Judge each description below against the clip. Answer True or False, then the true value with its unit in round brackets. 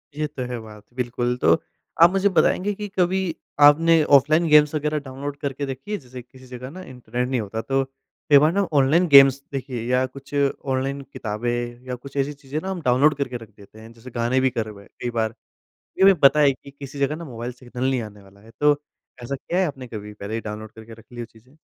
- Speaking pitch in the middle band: False (130 Hz)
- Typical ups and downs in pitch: True (3.5 semitones)